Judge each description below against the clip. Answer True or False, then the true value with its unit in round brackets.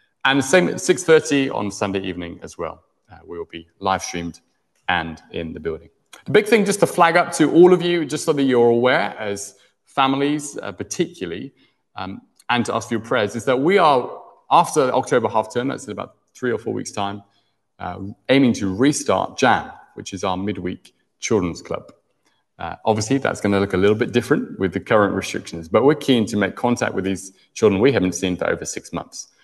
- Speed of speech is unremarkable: False (210 wpm)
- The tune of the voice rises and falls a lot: True (6.9 semitones)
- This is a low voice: True (110 Hz)